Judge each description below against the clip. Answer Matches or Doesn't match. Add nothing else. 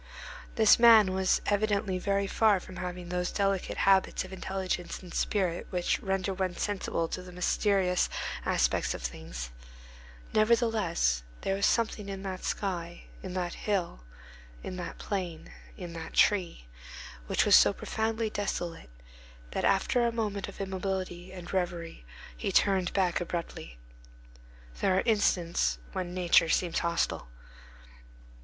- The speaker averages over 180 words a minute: Doesn't match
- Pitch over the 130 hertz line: Matches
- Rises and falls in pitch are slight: Matches